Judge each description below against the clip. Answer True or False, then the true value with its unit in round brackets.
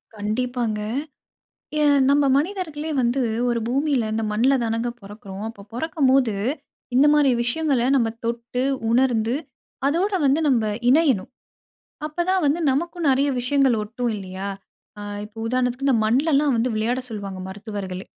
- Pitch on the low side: False (250 Hz)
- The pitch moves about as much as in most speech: True (4.2 semitones)